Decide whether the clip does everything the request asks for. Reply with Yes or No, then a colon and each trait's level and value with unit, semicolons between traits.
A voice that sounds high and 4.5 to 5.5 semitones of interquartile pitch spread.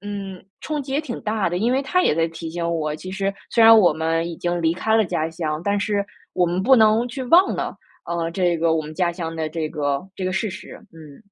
No: medium, 180 Hz; average, 4.8 semitones